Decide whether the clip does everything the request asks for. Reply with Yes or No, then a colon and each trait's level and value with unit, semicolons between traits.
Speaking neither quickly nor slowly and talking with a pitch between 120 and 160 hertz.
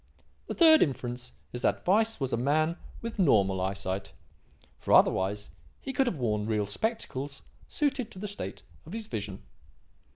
Yes: average, 160 wpm; low, 135 Hz